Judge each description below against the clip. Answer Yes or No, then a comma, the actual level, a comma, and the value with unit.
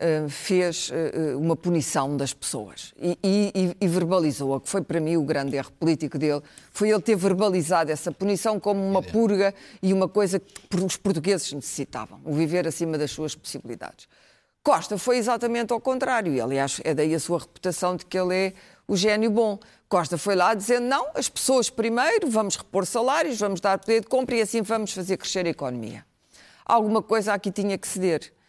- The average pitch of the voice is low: No, high, 190 Hz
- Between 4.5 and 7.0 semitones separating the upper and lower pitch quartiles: Yes, average, 4.8 semitones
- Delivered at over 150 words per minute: Yes, fast, 185 wpm